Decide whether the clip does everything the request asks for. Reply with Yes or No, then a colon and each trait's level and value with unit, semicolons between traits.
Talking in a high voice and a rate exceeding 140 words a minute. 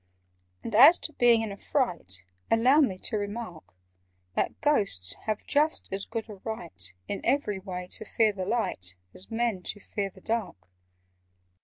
Yes: high, 210 Hz; average, 165 wpm